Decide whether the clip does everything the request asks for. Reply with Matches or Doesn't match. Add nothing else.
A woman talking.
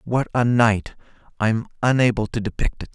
Doesn't match